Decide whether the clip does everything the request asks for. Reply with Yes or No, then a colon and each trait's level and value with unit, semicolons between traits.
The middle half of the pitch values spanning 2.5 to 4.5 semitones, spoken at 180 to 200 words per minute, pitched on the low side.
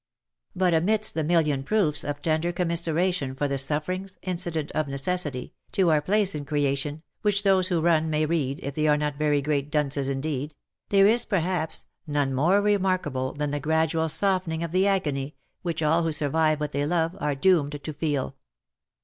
No: average, 3.6 semitones; average, 185 wpm; medium, 155 Hz